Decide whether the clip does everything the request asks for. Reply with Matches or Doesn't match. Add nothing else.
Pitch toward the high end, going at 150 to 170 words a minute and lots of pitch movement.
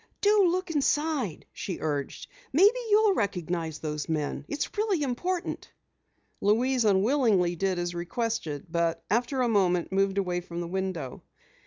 Doesn't match